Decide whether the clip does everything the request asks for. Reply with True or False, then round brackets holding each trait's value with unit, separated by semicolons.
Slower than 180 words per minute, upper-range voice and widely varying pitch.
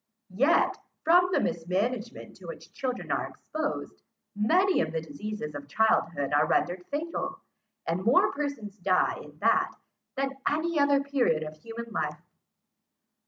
True (145 wpm; 230 Hz; 8.4 semitones)